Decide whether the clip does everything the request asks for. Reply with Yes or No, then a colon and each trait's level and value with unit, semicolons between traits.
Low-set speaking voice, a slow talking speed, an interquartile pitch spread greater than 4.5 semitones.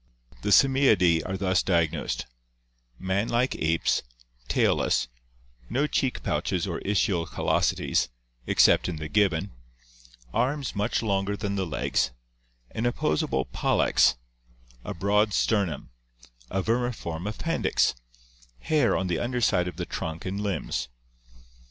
Yes: low, 100 Hz; slow, 120 wpm; average, 4.9 semitones